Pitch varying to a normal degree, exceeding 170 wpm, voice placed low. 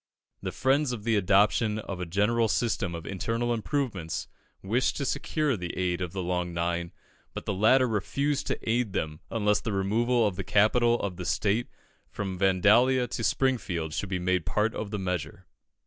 Yes: average, 4.5 semitones; average, 185 wpm; low, 105 Hz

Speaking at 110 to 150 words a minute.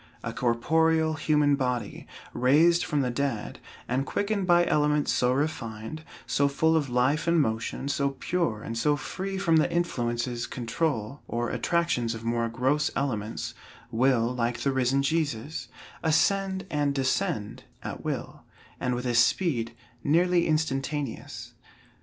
Yes: average, 140 wpm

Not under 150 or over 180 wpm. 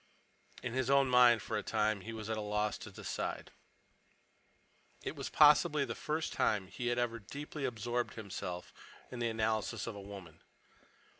Yes: average, 170 wpm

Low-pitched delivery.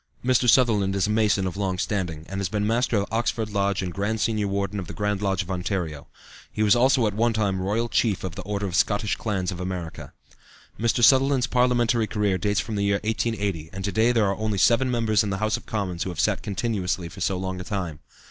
Yes: low, 100 Hz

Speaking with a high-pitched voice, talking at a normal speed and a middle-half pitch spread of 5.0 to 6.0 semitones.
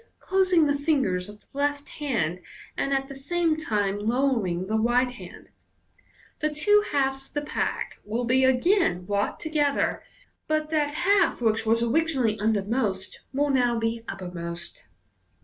Yes: very high, 260 Hz; average, 150 wpm; wide, 5.5 semitones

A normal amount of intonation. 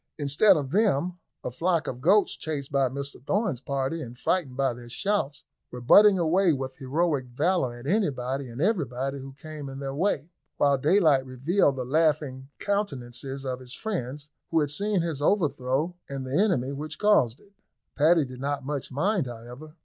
Yes: average, 4.6 semitones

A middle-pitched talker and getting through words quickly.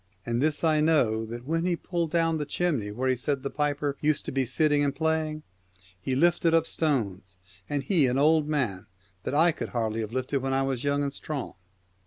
Yes: medium, 145 Hz; fast, 215 wpm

